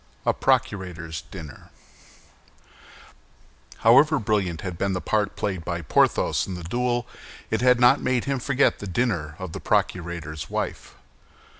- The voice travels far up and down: Yes, wide, 6.2 semitones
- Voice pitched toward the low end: Yes, very low, 95 Hz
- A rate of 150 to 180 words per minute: No, average, 140 wpm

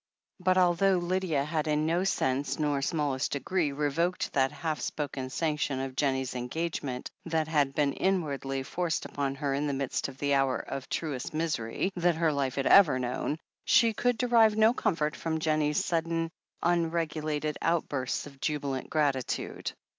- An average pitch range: Yes, average, 3.4 semitones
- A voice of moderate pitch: Yes, medium, 150 Hz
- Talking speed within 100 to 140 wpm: No, average, 160 wpm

